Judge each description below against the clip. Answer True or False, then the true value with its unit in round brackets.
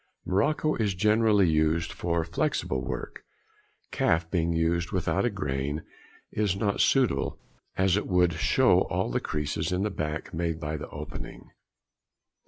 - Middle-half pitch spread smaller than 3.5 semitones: False (4.4 semitones)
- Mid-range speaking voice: False (85 Hz)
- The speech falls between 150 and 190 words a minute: False (140 wpm)